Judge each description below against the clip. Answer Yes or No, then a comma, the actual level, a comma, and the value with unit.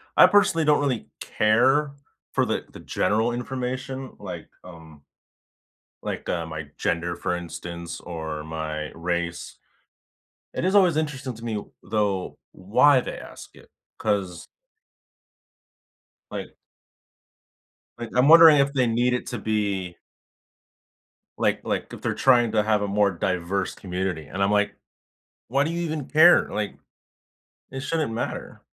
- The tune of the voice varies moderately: No, wide, 7.0 semitones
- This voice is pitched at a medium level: No, low, 110 Hz